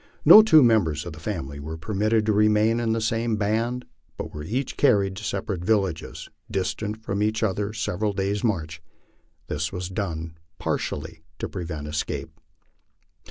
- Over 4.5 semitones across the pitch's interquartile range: Yes, average, 4.9 semitones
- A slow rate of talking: No, average, 160 wpm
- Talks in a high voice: No, low, 100 Hz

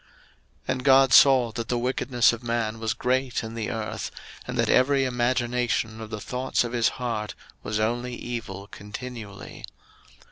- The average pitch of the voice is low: Yes, low, 120 Hz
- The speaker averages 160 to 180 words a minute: Yes, average, 165 wpm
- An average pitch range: No, narrow, 2.1 semitones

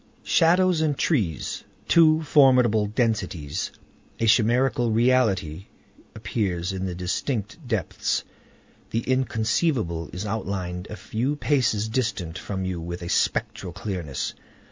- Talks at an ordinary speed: No, slow, 110 wpm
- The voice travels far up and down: Yes, wide, 5.8 semitones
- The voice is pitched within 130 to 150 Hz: No, low, 110 Hz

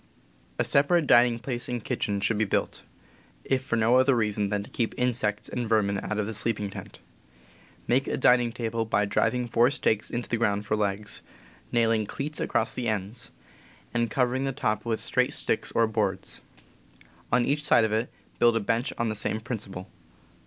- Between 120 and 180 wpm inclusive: No, average, 190 wpm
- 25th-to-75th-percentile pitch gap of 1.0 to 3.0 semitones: Yes, narrow, 2.5 semitones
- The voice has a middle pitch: No, low, 115 Hz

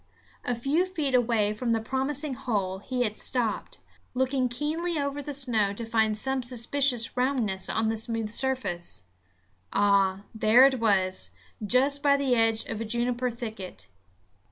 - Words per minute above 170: No, average, 155 wpm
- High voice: Yes, high, 240 Hz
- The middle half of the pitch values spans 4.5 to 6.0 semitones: No, average, 3.7 semitones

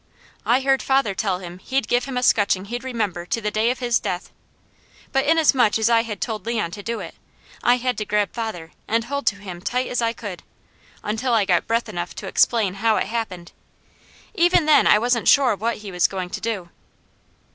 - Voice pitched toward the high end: Yes, high, 225 Hz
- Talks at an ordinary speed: No, fast, 210 wpm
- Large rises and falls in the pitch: No, average, 3.8 semitones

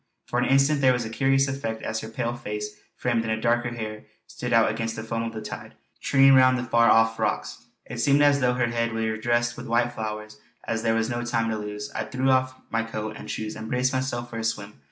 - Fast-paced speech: Yes, fast, 245 wpm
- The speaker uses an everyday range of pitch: No, narrow, 2.1 semitones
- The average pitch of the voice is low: Yes, low, 115 Hz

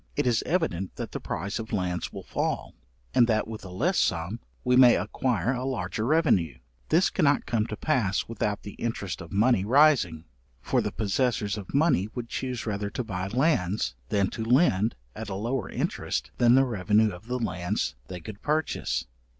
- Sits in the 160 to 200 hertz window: No, low, 110 Hz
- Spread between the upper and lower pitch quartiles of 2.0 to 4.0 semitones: No, average, 4.8 semitones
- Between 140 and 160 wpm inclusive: No, average, 185 wpm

